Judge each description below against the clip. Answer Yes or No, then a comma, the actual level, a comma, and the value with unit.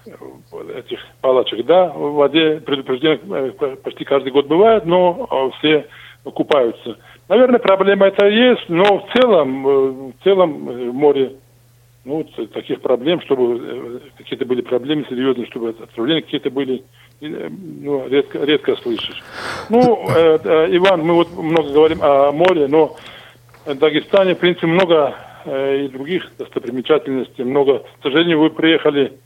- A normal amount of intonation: No, wide, 6.1 semitones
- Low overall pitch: No, medium, 155 Hz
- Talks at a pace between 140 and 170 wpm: No, average, 125 wpm